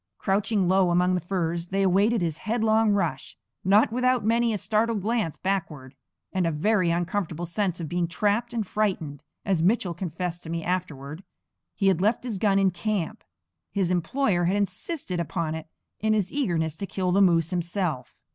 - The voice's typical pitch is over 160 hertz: Yes, medium, 185 Hz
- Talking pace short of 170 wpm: No, average, 175 wpm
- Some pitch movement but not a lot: Yes, average, 3.7 semitones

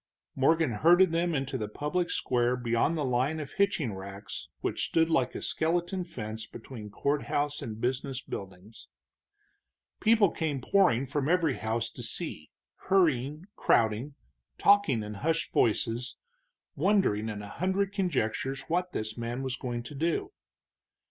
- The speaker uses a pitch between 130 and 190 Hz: Yes, low, 135 Hz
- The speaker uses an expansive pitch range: Yes, wide, 6.5 semitones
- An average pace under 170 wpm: Yes, average, 140 wpm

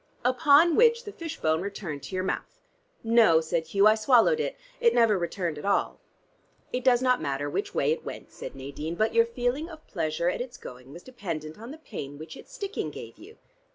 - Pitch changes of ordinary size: No, wide, 8.6 semitones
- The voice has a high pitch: Yes, high, 215 Hz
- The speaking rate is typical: No, fast, 210 wpm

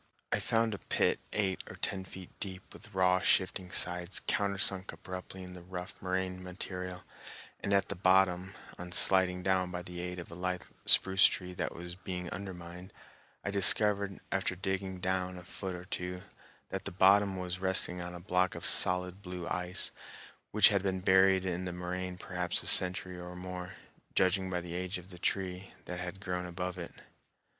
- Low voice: Yes, very low, 90 Hz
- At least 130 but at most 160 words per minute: No, average, 185 wpm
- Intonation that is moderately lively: No, narrow, 0.9 semitones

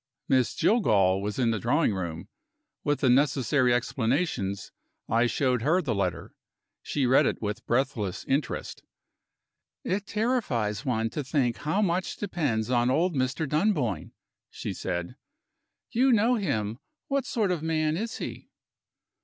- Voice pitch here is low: Yes, low, 130 Hz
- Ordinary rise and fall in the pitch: No, wide, 7.3 semitones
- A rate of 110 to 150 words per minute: Yes, average, 140 wpm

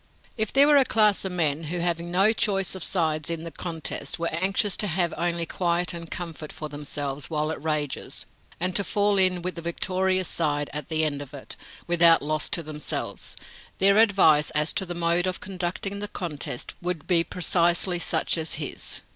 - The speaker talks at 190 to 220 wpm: Yes, average, 195 wpm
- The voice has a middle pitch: Yes, medium, 170 Hz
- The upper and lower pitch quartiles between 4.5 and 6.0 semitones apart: No, average, 3.1 semitones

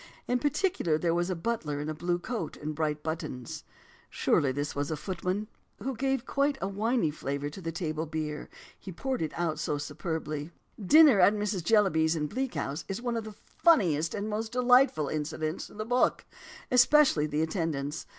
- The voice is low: No, medium, 170 Hz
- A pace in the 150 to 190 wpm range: Yes, average, 185 wpm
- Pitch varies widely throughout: Yes, wide, 6.8 semitones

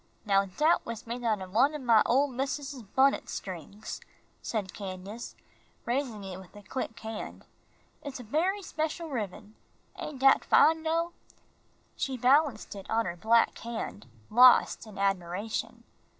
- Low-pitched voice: No, high, 230 Hz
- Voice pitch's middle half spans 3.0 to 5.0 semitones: No, wide, 5.5 semitones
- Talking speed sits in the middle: Yes, average, 150 wpm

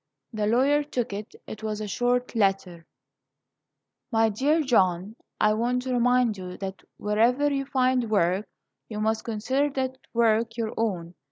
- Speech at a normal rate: Yes, average, 155 wpm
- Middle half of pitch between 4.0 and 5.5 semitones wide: No, average, 3.2 semitones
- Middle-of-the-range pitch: No, high, 225 Hz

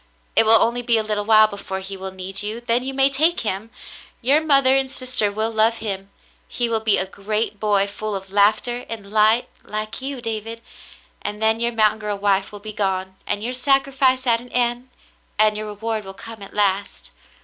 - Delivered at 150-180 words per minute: No, fast, 205 wpm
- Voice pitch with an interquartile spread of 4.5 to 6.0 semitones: No, average, 2.8 semitones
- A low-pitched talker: No, high, 220 Hz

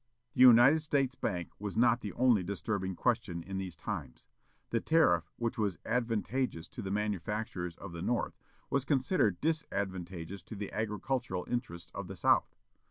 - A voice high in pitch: No, low, 105 Hz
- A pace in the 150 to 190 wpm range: Yes, average, 160 wpm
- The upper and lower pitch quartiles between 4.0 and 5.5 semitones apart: Yes, average, 5.1 semitones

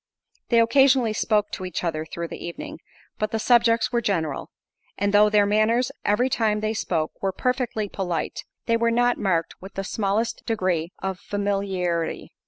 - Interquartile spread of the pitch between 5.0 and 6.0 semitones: No, average, 3.7 semitones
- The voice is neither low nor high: No, high, 210 Hz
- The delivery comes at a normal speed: Yes, average, 165 wpm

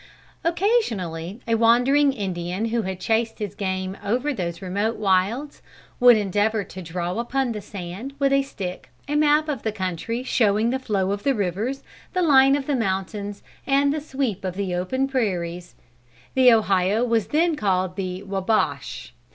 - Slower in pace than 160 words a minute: No, average, 165 wpm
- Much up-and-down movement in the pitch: Yes, wide, 5.9 semitones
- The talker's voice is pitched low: No, high, 220 Hz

